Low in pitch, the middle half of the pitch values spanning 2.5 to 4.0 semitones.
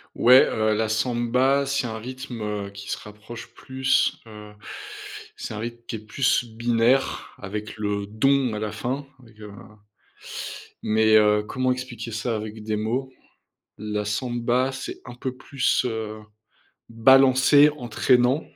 Yes: low, 115 Hz; average, 3.1 semitones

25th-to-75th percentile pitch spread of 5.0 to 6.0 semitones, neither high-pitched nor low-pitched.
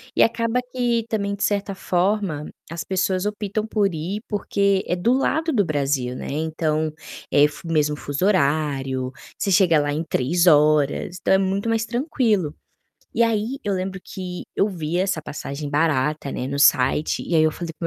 Yes: average, 5.3 semitones; medium, 180 Hz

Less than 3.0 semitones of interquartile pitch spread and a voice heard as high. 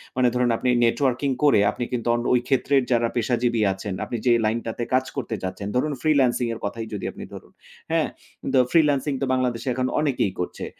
No: narrow, 2.6 semitones; low, 125 Hz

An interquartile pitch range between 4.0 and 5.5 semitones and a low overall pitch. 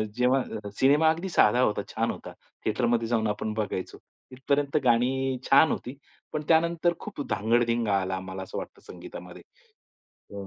Yes: average, 4.7 semitones; low, 125 Hz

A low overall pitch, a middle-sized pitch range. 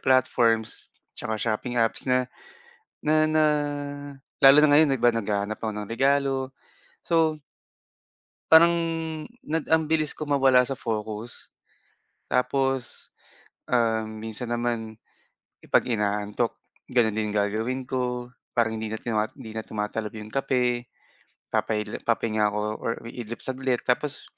Yes: low, 120 Hz; average, 3.3 semitones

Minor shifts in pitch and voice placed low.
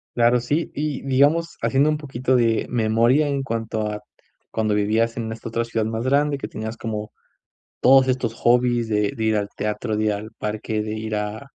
No: average, 3.2 semitones; low, 115 Hz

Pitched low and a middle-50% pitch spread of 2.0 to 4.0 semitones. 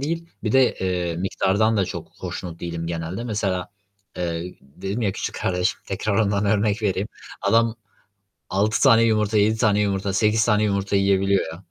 Yes: low, 100 Hz; average, 2.7 semitones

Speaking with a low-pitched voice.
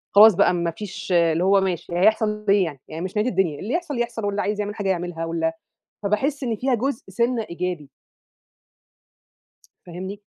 No: high, 200 Hz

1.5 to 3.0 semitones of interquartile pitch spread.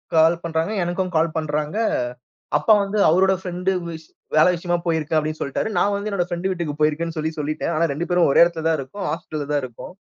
Yes: narrow, 2.5 semitones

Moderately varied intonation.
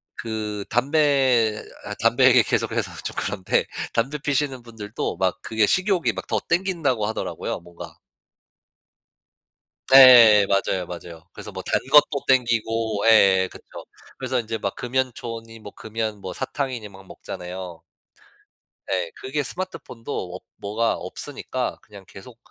Yes: average, 4.4 semitones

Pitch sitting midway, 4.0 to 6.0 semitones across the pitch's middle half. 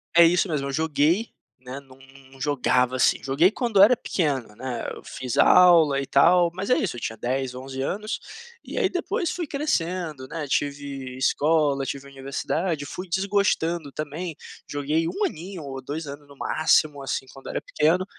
Yes: medium, 150 Hz; average, 4.6 semitones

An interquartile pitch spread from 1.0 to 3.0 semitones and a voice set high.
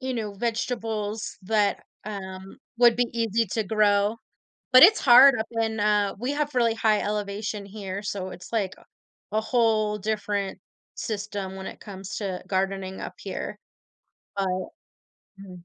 Yes: narrow, 2.4 semitones; high, 210 Hz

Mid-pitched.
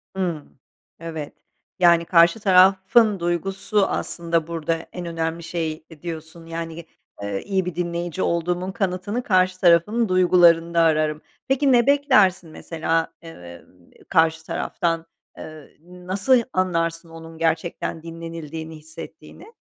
Yes: medium, 170 Hz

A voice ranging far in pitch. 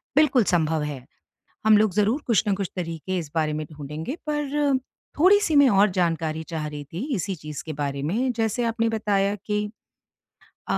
Yes: wide, 6.8 semitones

